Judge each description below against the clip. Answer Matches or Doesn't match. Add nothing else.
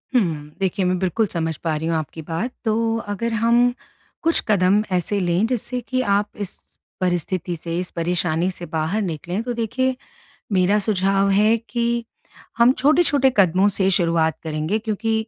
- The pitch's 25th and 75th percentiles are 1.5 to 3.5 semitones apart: Doesn't match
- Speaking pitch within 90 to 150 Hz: Doesn't match